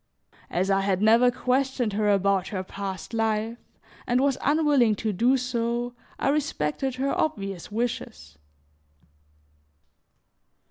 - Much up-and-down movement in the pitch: No, average, 4.5 semitones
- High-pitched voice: Yes, high, 230 Hz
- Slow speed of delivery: Yes, slow, 120 wpm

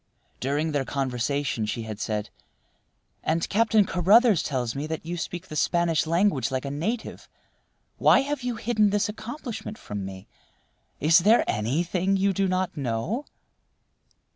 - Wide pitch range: Yes, wide, 7.4 semitones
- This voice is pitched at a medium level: Yes, medium, 165 Hz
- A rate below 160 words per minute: Yes, average, 145 wpm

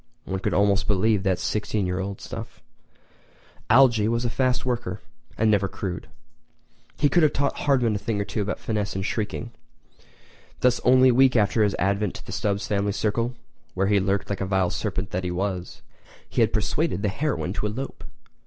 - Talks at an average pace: Yes, average, 190 wpm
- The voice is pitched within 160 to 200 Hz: No, low, 105 Hz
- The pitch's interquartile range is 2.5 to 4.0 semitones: Yes, average, 3.3 semitones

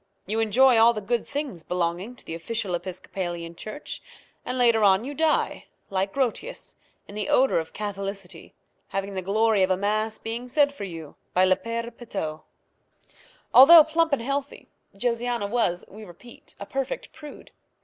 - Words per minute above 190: No, average, 165 wpm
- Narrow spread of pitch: No, average, 4.7 semitones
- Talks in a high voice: Yes, high, 215 Hz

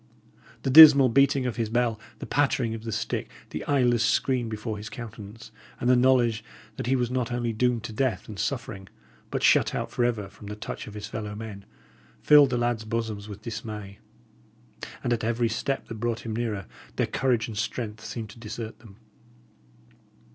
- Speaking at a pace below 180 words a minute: No, average, 190 wpm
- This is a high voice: No, low, 115 Hz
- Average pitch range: No, narrow, 2.3 semitones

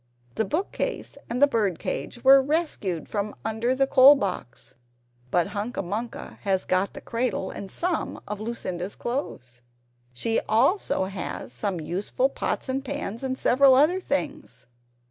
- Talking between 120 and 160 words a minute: Yes, average, 150 wpm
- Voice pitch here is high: Yes, high, 230 Hz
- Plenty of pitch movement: Yes, wide, 5.8 semitones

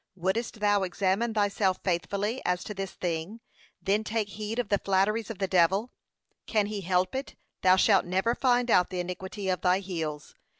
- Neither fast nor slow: Yes, average, 180 wpm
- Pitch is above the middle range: Yes, high, 195 Hz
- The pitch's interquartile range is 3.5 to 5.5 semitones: No, average, 2.7 semitones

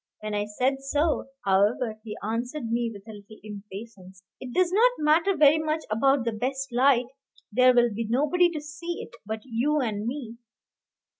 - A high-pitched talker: Yes, high, 245 Hz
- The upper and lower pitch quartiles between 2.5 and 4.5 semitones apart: No, wide, 5.4 semitones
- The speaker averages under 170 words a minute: No, average, 175 wpm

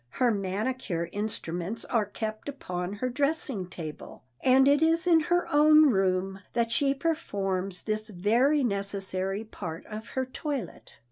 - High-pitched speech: Yes, high, 220 Hz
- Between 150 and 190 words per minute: No, average, 140 wpm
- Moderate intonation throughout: No, wide, 6.1 semitones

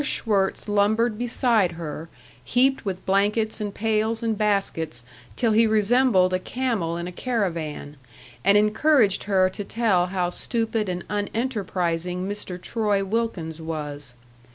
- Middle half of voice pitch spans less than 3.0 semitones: No, average, 4.0 semitones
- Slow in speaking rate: Yes, slow, 130 wpm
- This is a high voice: Yes, high, 205 Hz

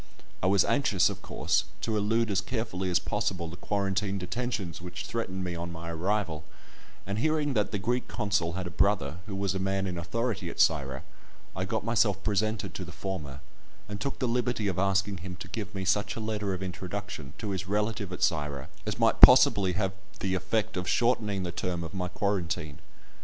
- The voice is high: No, very low, 95 Hz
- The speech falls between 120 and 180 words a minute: No, average, 200 wpm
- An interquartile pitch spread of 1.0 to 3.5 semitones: Yes, average, 2.9 semitones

